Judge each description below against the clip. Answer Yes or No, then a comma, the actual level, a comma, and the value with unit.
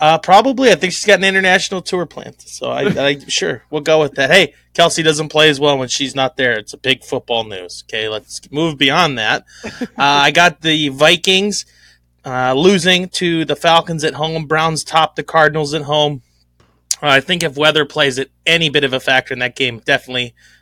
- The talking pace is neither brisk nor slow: No, fast, 210 wpm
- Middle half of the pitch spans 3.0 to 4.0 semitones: Yes, average, 3.6 semitones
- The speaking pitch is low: No, medium, 155 Hz